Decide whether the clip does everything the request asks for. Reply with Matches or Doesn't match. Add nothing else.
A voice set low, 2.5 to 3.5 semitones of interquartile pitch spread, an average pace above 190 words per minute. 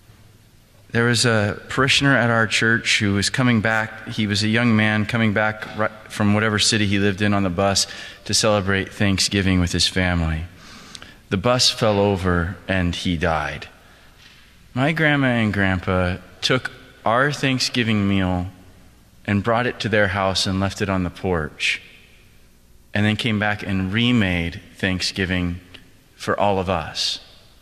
Doesn't match